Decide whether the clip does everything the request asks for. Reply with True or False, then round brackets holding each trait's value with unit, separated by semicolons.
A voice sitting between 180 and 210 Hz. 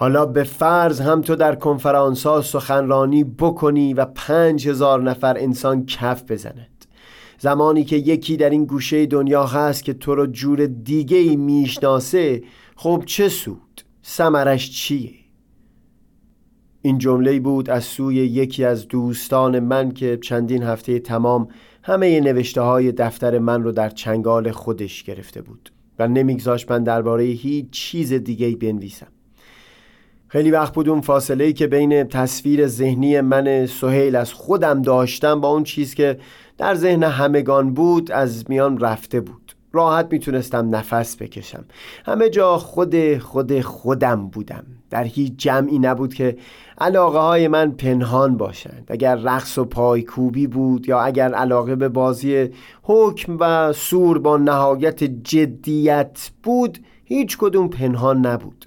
False (135 Hz)